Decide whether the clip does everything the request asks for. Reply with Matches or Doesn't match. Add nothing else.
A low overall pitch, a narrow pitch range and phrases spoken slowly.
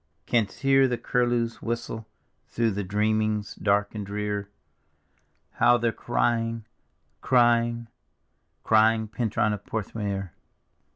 Matches